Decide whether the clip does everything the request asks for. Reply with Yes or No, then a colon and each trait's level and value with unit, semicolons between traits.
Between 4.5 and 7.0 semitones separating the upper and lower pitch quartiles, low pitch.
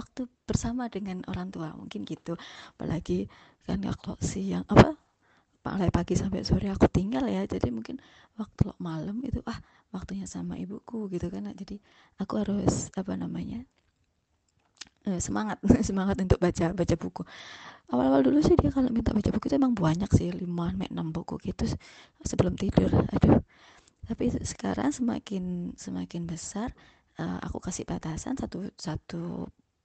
No: average, 5.1 semitones; high, 190 Hz